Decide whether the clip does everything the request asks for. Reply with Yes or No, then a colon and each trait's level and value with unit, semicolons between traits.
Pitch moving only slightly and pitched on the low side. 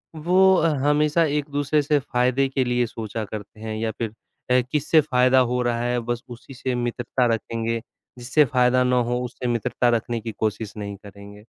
No: average, 3.1 semitones; low, 125 Hz